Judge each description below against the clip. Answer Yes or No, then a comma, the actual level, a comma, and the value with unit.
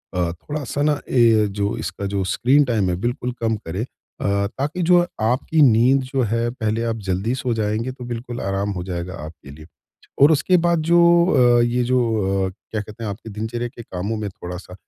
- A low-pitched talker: Yes, low, 115 Hz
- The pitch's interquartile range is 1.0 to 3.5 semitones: No, average, 4.1 semitones